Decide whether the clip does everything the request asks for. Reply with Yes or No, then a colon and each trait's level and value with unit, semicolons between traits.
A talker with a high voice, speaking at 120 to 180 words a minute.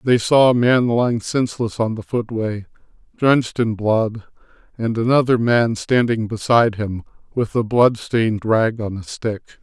No: low, 115 Hz; average, 160 wpm